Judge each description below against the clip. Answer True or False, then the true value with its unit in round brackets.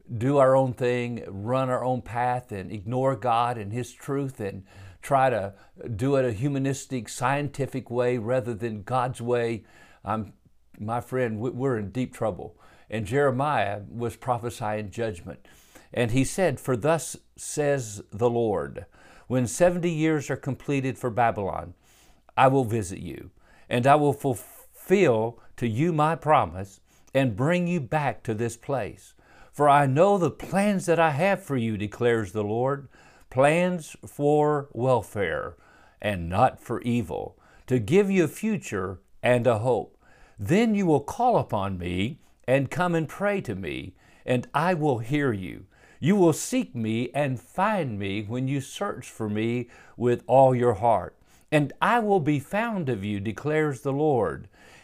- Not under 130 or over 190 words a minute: True (160 wpm)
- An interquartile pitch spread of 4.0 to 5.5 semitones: True (4.3 semitones)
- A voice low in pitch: True (125 Hz)